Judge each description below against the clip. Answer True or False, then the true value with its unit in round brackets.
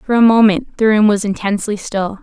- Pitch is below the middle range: False (210 Hz)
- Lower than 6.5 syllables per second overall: True (5.5 syllables/s)